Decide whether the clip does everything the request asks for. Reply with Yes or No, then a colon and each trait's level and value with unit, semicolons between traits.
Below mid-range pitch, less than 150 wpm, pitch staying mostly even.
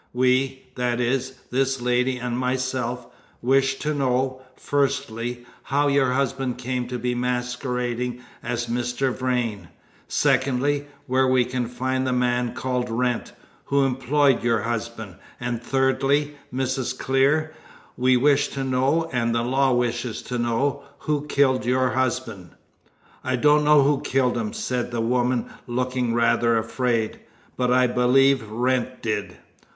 Yes: low, 125 Hz; average, 140 wpm; narrow, 1.7 semitones